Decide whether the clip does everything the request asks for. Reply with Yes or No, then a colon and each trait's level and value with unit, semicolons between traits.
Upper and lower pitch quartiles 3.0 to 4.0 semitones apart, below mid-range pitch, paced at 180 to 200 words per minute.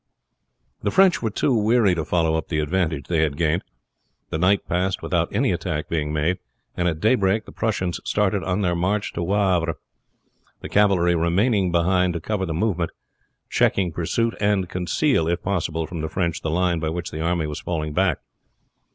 Yes: average, 3.4 semitones; very low, 90 Hz; average, 185 wpm